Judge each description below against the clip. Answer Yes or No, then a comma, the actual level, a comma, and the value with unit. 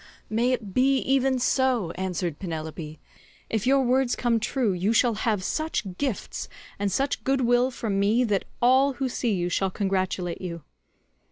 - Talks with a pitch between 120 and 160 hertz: No, high, 225 Hz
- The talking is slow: No, average, 165 wpm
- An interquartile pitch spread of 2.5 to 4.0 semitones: No, wide, 5.5 semitones